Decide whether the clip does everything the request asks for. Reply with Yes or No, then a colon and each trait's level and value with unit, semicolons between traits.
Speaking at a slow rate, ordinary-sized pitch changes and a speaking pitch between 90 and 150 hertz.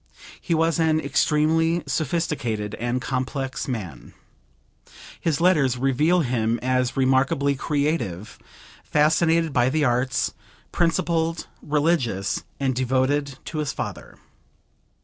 Yes: slow, 105 wpm; average, 4.1 semitones; medium, 140 Hz